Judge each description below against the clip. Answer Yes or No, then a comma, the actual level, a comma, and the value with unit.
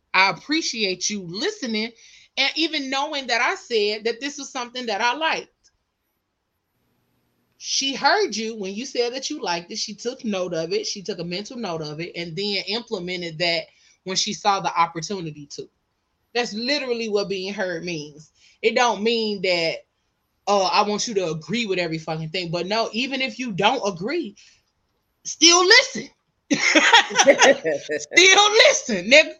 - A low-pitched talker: No, high, 220 Hz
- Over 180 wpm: No, average, 165 wpm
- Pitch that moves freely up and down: Yes, wide, 6.1 semitones